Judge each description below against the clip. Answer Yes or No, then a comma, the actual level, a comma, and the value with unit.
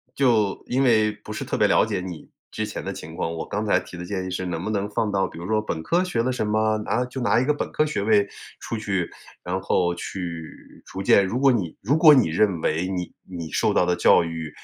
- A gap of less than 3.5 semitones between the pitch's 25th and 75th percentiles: No, average, 4.4 semitones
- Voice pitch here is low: Yes, low, 100 Hz